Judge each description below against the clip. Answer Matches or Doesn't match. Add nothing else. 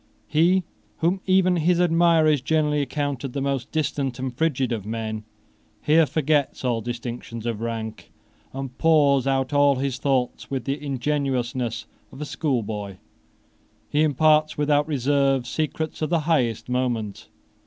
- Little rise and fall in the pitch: Doesn't match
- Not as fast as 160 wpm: Matches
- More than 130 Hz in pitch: Matches